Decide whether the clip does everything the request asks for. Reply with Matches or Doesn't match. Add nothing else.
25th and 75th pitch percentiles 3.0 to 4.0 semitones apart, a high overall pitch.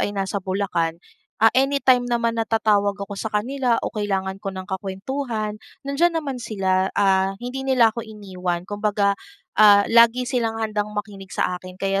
Matches